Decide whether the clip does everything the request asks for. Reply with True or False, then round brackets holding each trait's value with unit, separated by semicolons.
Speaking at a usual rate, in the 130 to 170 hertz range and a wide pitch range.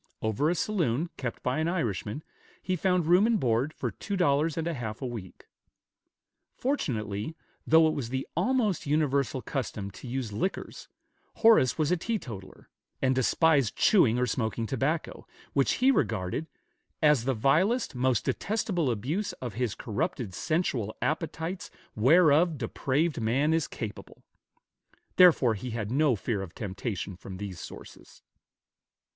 True (145 wpm; 135 Hz; 6.5 semitones)